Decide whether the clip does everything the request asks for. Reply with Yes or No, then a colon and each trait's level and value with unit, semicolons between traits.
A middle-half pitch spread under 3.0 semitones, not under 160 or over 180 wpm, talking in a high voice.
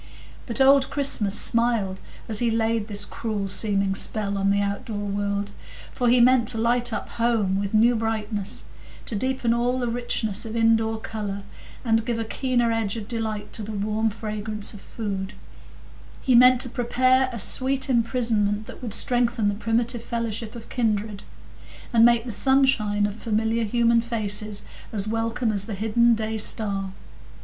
Yes: narrow, 2.4 semitones; average, 165 wpm; high, 225 Hz